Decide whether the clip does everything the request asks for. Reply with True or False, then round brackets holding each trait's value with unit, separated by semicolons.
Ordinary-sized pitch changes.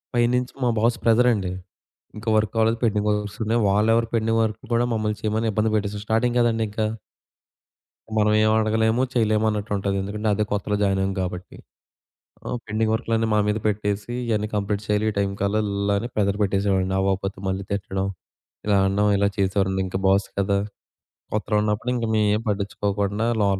False (1.9 semitones)